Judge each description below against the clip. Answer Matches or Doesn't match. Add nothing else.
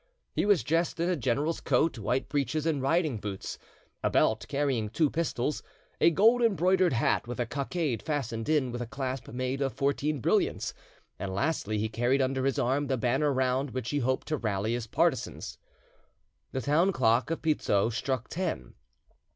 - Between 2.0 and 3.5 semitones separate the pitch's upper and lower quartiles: Doesn't match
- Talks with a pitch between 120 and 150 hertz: Matches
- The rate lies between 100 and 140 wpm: Doesn't match